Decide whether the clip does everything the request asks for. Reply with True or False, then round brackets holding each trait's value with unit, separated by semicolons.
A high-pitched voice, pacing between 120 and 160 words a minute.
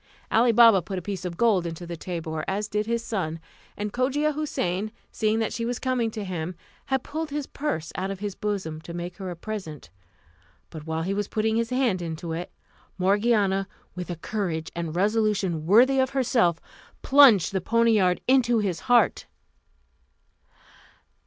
False (200 Hz; 175 wpm)